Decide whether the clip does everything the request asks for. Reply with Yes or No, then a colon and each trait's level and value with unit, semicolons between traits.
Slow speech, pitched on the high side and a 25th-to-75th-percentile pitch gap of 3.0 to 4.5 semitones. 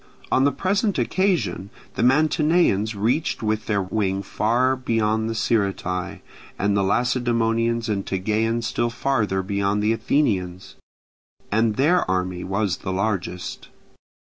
No: slow, 125 wpm; low, 110 Hz; average, 3.8 semitones